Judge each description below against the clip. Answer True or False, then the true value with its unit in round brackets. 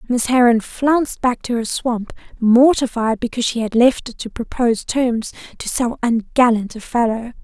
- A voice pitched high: True (240 Hz)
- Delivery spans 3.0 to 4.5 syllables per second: False (4.8 syllables/s)